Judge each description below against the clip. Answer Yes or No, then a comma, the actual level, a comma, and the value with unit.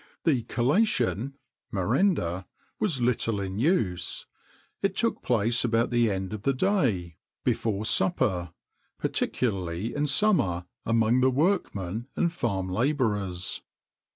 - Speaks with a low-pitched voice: Yes, low, 115 Hz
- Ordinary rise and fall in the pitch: No, wide, 6.5 semitones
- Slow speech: Yes, slow, 125 wpm